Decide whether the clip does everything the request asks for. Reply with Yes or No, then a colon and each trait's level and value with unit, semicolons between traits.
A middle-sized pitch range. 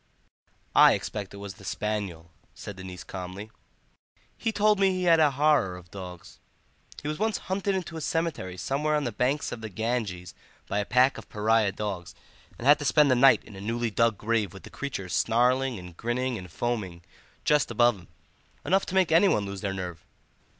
No: wide, 7.2 semitones